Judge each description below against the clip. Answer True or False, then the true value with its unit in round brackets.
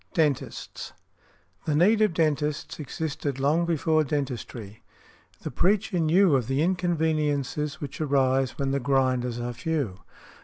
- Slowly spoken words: True (125 wpm)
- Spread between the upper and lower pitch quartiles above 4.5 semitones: False (3.3 semitones)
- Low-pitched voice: False (145 Hz)